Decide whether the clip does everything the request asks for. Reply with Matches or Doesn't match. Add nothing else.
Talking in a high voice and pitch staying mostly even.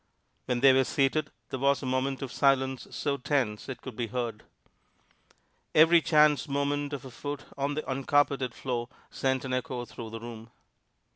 Doesn't match